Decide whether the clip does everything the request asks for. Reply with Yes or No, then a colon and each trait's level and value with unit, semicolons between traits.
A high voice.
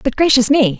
Yes: very high, 250 Hz